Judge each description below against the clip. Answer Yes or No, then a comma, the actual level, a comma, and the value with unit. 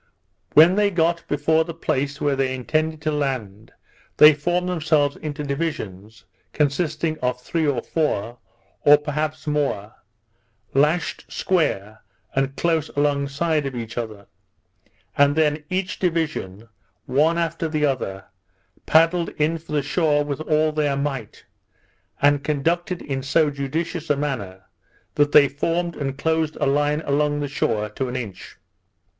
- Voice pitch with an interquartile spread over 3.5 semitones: No, average, 2.7 semitones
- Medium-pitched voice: Yes, medium, 145 Hz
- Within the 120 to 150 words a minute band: Yes, average, 145 wpm